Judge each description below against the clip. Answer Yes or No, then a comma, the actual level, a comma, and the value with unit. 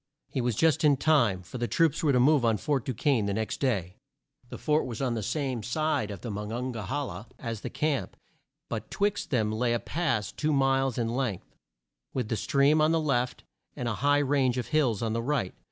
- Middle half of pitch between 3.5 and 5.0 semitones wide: Yes, average, 4.5 semitones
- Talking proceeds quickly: Yes, fast, 230 wpm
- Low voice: Yes, low, 125 Hz